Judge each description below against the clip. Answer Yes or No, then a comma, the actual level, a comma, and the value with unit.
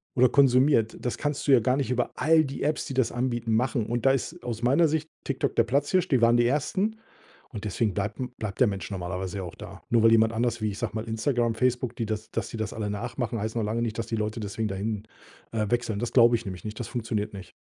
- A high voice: No, low, 115 Hz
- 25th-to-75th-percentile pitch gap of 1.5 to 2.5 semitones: No, average, 2.9 semitones